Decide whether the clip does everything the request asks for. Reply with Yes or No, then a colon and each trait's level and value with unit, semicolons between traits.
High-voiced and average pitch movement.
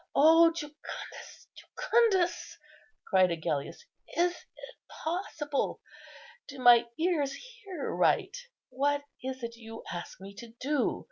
No: very high, 285 Hz; wide, 6.6 semitones